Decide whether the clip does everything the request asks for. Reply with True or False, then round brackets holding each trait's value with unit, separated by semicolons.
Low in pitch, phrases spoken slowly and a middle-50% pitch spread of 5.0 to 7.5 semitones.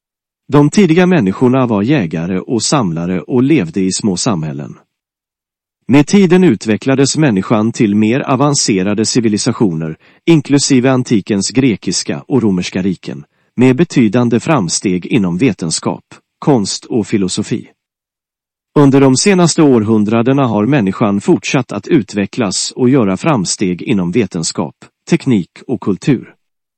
True (125 Hz; 115 wpm; 5.5 semitones)